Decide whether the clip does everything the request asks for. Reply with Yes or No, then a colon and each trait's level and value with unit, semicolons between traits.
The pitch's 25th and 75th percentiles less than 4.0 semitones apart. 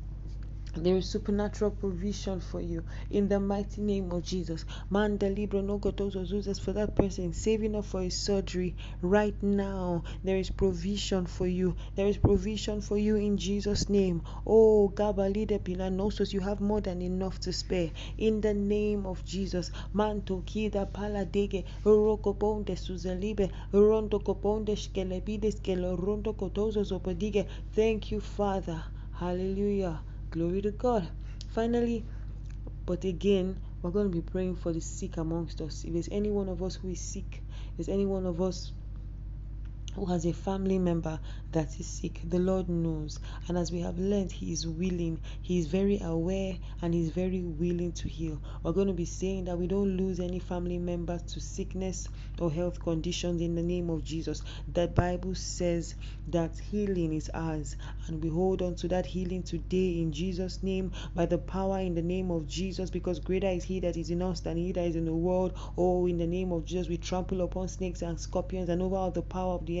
Yes: average, 2.9 semitones